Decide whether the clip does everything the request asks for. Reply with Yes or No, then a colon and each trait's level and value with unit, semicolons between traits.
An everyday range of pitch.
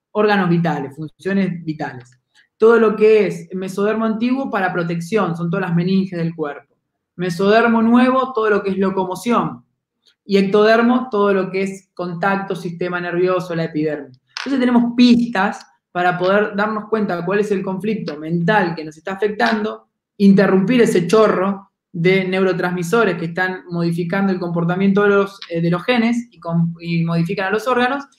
Yes: average, 3.4 semitones